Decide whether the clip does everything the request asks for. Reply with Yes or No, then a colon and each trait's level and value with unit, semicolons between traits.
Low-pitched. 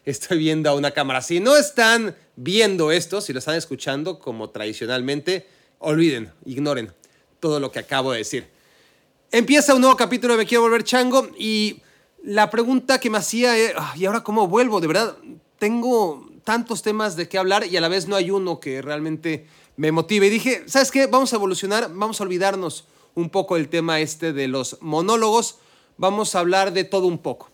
No: high, 190 Hz